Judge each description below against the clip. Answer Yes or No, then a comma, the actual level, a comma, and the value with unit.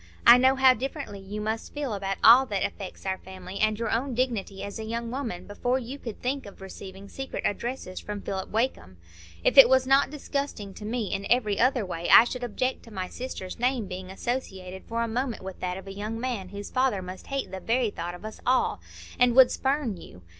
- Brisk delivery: Yes, fast, 220 wpm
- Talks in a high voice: Yes, high, 225 Hz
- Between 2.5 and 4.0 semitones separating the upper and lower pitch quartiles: No, average, 4.8 semitones